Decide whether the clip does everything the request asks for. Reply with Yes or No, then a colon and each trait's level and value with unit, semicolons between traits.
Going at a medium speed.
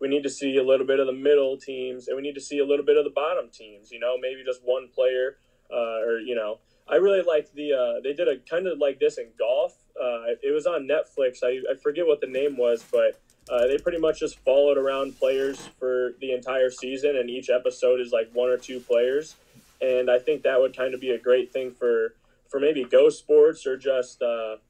No: fast, 245 wpm